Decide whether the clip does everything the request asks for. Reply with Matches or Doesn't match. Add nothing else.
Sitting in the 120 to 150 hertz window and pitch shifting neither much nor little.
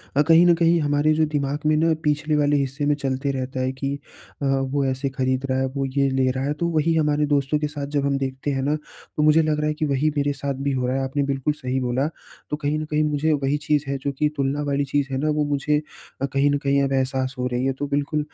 Doesn't match